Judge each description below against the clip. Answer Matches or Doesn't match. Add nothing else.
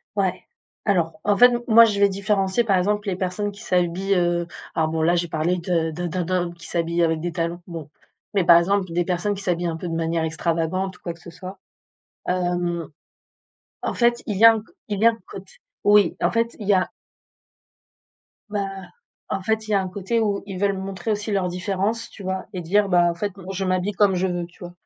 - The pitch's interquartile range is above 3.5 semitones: Doesn't match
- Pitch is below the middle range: Doesn't match